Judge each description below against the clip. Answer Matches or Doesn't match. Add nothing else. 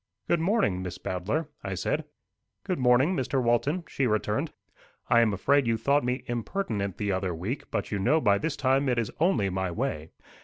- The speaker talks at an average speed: Matches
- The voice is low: Matches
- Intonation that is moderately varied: Doesn't match